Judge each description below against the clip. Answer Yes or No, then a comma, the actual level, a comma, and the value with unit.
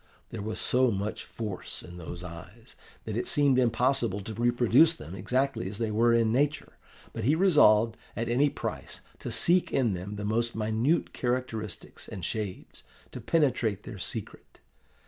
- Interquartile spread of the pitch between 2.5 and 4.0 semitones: Yes, average, 3.7 semitones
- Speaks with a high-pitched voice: No, low, 115 Hz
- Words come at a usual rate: Yes, average, 165 wpm